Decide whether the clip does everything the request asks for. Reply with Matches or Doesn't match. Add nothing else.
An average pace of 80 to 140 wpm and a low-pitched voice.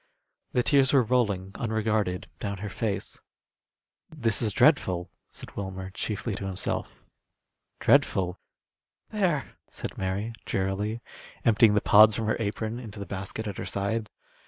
Matches